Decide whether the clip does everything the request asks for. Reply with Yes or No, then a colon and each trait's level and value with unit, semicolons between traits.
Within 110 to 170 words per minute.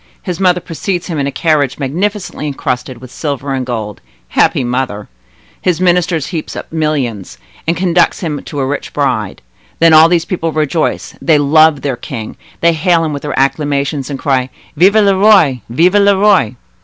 No: average, 180 wpm